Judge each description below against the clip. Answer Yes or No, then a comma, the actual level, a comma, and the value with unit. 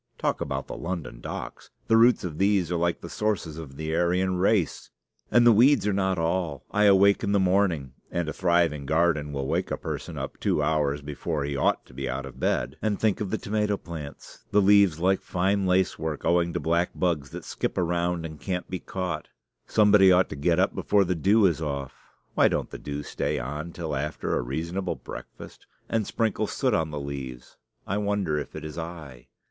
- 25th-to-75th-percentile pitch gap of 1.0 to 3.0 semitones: No, average, 4.5 semitones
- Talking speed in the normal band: No, fast, 210 wpm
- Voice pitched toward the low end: Yes, very low, 85 Hz